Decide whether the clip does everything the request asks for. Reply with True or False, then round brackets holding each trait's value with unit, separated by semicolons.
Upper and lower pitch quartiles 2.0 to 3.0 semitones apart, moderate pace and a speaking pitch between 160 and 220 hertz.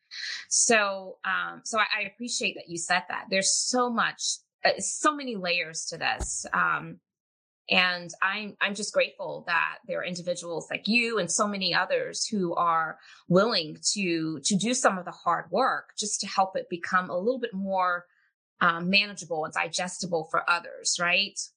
False (3.7 semitones; 165 wpm; 190 Hz)